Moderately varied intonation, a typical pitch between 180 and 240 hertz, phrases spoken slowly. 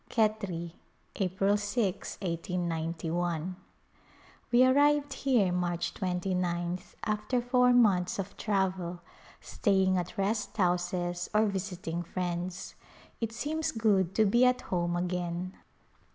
Yes: average, 3.5 semitones; medium, 185 Hz; slow, 110 wpm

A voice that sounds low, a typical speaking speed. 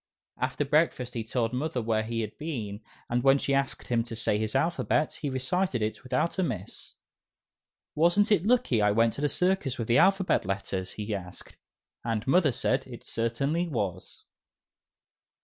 Yes: low, 125 Hz; average, 170 wpm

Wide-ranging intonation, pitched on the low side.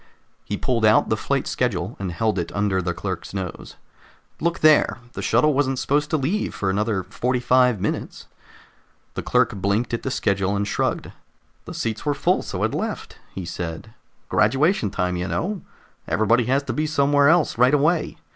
Yes: wide, 6.4 semitones; low, 115 Hz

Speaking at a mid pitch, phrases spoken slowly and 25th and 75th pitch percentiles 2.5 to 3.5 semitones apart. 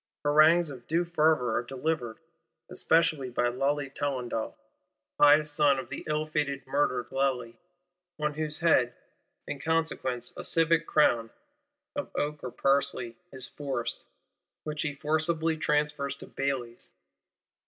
Yes: medium, 145 Hz; slow, 125 wpm; average, 3.1 semitones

